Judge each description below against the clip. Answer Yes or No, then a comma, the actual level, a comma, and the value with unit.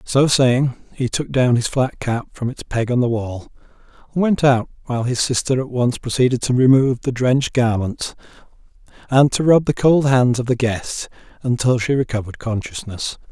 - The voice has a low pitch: Yes, low, 125 Hz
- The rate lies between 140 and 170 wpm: No, average, 185 wpm